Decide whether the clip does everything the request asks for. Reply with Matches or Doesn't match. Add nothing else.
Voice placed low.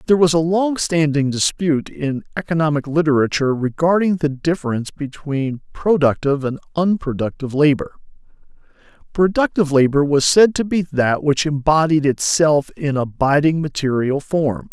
Doesn't match